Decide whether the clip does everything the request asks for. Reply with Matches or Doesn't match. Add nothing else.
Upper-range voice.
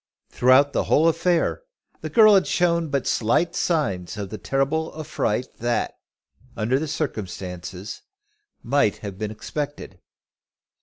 Doesn't match